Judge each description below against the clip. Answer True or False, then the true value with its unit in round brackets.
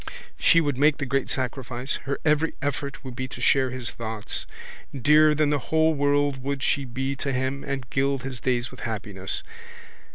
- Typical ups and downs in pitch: False (2.1 semitones)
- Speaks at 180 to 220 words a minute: True (185 wpm)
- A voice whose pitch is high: False (135 Hz)